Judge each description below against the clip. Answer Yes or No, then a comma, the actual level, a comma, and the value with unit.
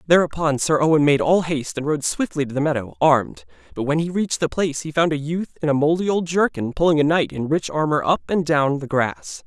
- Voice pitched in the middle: Yes, medium, 155 Hz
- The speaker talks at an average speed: No, fast, 245 wpm